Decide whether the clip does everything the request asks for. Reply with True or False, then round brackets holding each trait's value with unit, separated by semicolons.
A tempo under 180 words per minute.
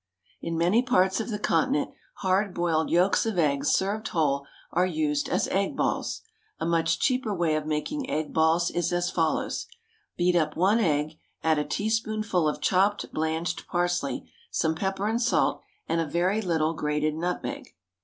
True (165 wpm)